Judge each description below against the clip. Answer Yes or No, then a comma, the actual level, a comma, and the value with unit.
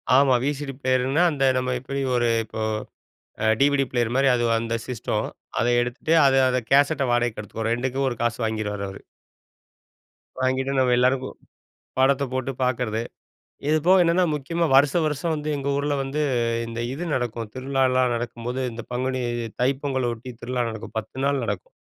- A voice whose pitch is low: Yes, low, 130 Hz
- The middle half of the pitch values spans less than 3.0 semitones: Yes, narrow, 2.5 semitones